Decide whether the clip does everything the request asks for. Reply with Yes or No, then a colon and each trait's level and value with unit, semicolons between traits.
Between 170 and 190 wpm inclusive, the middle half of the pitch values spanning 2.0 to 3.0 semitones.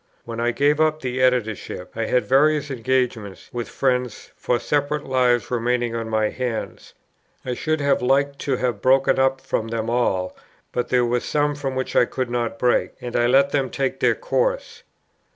Yes: average, 180 wpm; narrow, 2.5 semitones